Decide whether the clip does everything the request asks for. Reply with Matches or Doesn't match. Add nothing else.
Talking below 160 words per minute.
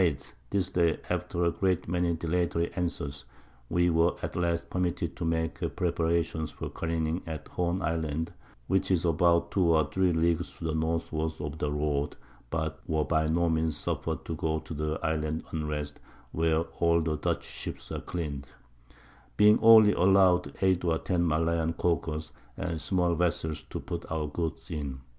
Doesn't match